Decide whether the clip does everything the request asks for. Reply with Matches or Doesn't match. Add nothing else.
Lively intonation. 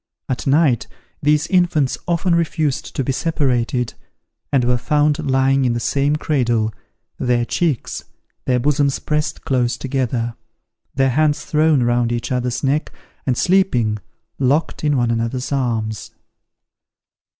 Doesn't match